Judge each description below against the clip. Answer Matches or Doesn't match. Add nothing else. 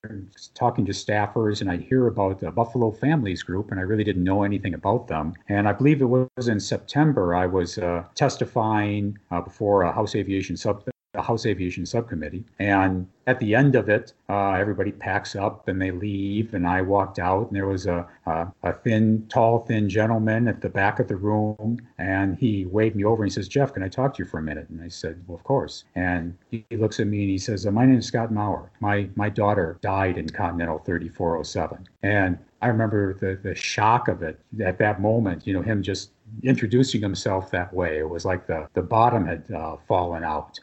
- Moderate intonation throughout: Matches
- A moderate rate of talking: Doesn't match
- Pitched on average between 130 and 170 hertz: Doesn't match